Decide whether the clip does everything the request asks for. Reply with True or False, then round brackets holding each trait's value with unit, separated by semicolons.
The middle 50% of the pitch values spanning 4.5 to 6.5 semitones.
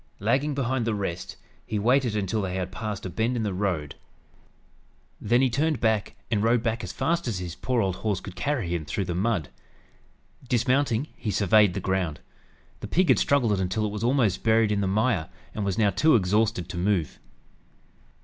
False (4.0 semitones)